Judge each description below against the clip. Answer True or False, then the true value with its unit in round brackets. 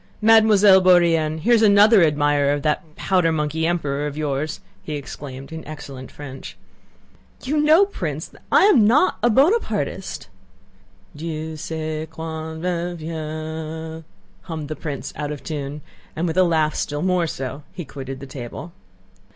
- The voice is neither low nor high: True (160 Hz)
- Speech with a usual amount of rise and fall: True (3.4 semitones)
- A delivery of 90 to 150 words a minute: True (145 wpm)